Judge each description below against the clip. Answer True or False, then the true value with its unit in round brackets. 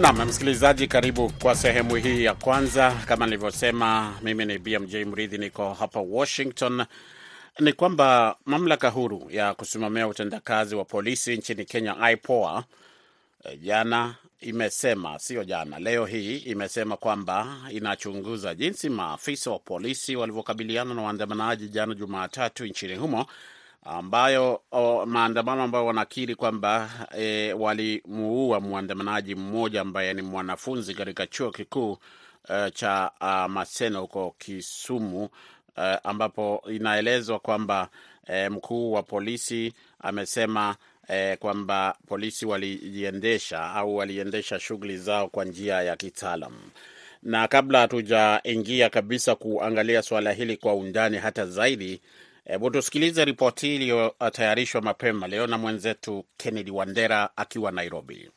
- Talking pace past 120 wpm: False (115 wpm)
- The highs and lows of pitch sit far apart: False (2.6 semitones)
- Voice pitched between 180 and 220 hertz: False (110 Hz)